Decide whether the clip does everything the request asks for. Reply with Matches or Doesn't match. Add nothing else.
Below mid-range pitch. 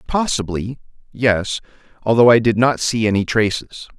Matches